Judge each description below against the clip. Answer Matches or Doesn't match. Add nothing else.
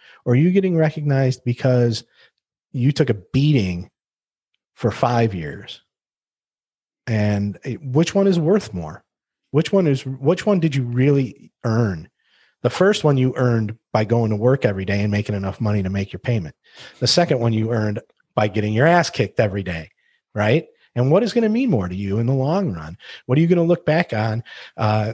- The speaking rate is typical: Matches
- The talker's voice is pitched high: Doesn't match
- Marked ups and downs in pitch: Matches